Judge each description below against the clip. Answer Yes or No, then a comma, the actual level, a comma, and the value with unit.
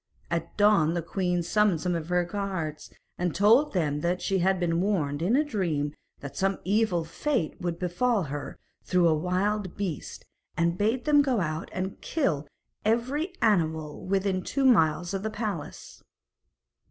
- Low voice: No, medium, 185 Hz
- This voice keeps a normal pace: Yes, average, 165 wpm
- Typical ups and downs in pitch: Yes, average, 4.1 semitones